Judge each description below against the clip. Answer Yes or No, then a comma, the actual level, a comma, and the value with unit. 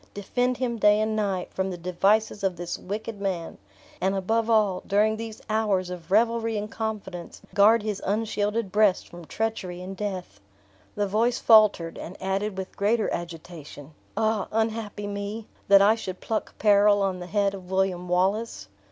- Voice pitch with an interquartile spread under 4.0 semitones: Yes, average, 2.8 semitones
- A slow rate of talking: No, average, 165 wpm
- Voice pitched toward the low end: No, high, 205 Hz